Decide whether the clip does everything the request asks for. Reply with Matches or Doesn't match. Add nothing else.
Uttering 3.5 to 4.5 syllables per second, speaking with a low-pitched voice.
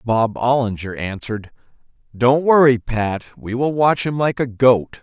Matches